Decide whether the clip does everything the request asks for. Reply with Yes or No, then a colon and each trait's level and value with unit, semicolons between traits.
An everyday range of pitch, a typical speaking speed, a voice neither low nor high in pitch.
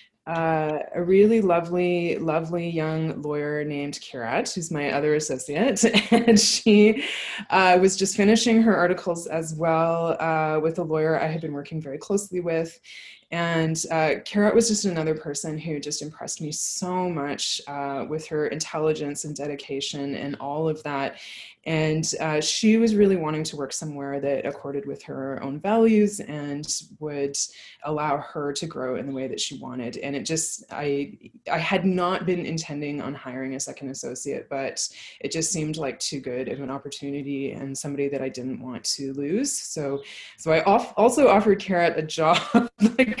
Yes: average, 4.1 semitones; average, 175 wpm; medium, 155 Hz